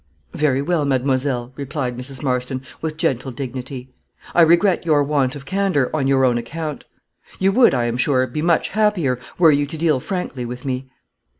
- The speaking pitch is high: No, medium, 140 Hz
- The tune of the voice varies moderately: Yes, average, 3.8 semitones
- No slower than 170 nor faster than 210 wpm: Yes, average, 180 wpm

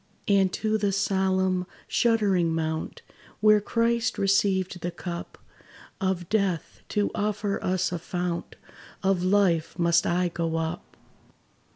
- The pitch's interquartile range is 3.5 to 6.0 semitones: No, average, 2.7 semitones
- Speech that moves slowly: Yes, slow, 125 wpm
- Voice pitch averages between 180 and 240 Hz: Yes, high, 190 Hz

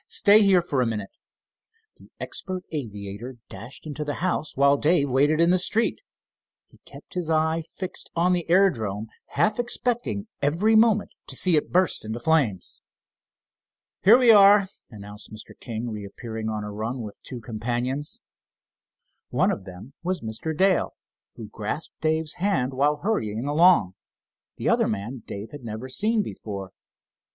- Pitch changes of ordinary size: No, wide, 8.5 semitones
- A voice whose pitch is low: No, medium, 145 Hz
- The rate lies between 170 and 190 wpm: No, average, 155 wpm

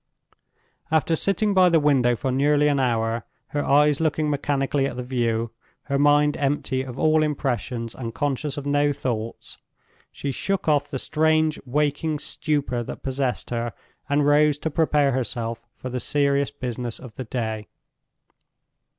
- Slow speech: No, average, 155 wpm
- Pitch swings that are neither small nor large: Yes, average, 3.1 semitones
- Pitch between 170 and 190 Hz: No, medium, 140 Hz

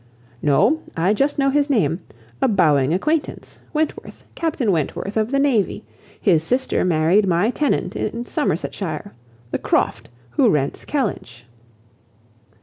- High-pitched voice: Yes, high, 210 Hz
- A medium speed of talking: No, slow, 130 wpm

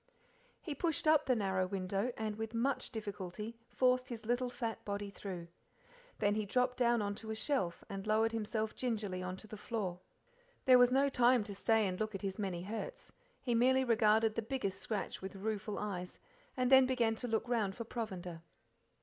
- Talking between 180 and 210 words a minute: Yes, average, 190 wpm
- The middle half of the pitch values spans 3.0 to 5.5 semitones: Yes, average, 3.6 semitones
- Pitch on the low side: No, high, 220 Hz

